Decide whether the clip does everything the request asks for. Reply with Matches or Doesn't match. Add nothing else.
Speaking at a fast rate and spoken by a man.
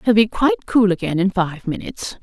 Doesn't match